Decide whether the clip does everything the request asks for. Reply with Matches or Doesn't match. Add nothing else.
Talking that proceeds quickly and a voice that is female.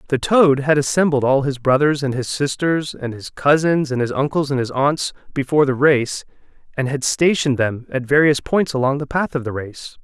Doesn't match